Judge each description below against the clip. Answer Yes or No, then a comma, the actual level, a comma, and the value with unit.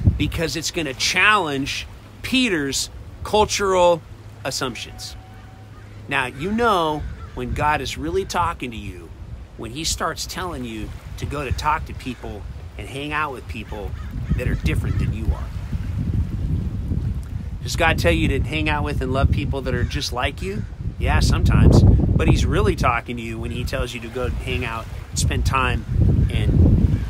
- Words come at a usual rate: Yes, average, 165 wpm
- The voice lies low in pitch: Yes, low, 110 Hz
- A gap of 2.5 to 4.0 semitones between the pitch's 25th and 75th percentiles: No, average, 4.7 semitones